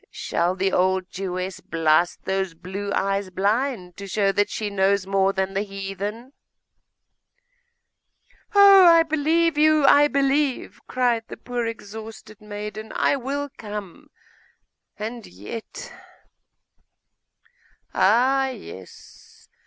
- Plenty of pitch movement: Yes, wide, 5.8 semitones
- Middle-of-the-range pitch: No, high, 210 Hz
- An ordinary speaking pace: No, slow, 115 wpm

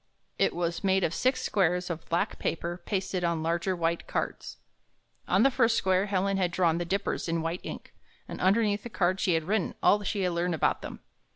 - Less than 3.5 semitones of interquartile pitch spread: Yes, narrow, 2.6 semitones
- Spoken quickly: Yes, fast, 210 wpm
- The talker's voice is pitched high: No, medium, 180 Hz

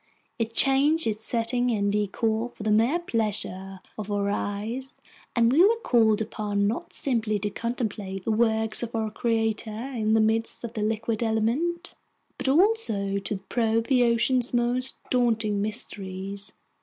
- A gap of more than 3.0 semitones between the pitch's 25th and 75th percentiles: No, narrow, 2.5 semitones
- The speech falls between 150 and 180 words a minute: Yes, average, 155 wpm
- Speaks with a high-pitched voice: Yes, high, 225 Hz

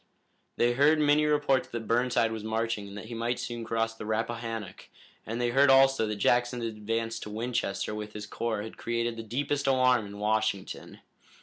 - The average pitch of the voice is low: Yes, low, 115 Hz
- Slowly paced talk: No, average, 185 wpm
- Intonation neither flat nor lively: No, narrow, 2.1 semitones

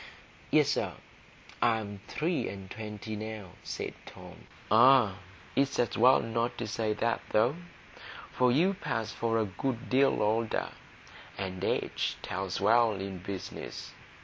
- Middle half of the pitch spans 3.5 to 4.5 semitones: No, average, 3.1 semitones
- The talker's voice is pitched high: No, low, 110 Hz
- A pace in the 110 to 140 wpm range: Yes, slow, 135 wpm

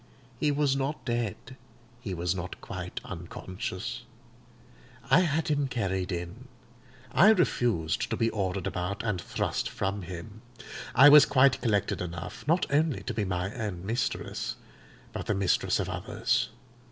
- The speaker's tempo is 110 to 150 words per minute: Yes, average, 145 wpm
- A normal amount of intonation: No, wide, 6.8 semitones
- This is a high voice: No, low, 105 Hz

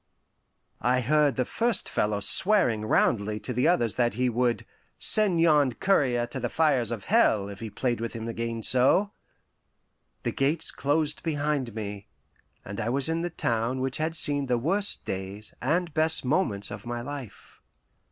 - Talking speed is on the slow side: No, average, 165 wpm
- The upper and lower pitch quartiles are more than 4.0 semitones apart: Yes, wide, 5.4 semitones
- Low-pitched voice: Yes, low, 125 Hz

